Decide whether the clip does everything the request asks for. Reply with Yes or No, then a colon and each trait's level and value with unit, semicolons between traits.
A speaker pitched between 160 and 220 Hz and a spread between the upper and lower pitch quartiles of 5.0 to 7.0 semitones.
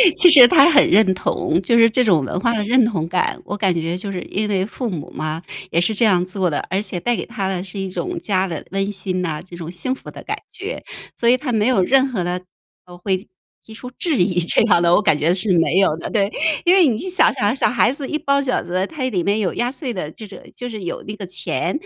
Yes: high, 200 Hz; wide, 5.4 semitones